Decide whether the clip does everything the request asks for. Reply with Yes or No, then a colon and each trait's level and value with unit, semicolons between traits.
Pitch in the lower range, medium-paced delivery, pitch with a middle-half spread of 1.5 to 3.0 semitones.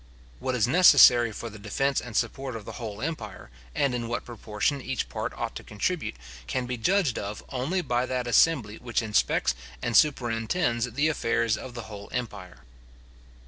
No: low, 120 Hz; average, 180 wpm; average, 3.5 semitones